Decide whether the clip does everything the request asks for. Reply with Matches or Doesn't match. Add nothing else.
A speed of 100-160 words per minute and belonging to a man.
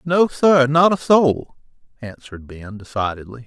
Matches